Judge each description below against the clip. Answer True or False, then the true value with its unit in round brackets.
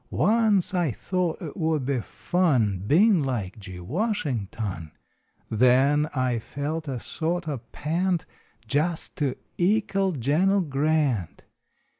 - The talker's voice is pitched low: False (150 Hz)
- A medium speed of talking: False (120 wpm)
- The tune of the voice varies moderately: False (6.1 semitones)